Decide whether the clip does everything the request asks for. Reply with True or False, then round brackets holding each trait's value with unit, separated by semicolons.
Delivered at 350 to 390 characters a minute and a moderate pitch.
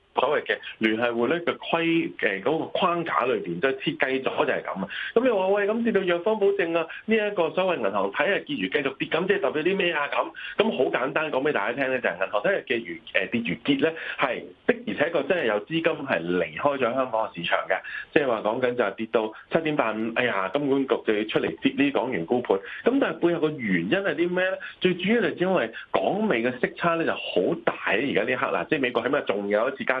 True (360 characters per minute; 165 Hz)